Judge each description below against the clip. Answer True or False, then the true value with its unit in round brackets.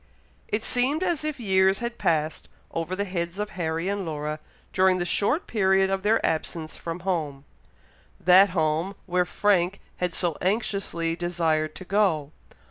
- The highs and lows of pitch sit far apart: False (3.4 semitones)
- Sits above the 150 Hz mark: True (185 Hz)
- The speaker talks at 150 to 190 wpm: True (155 wpm)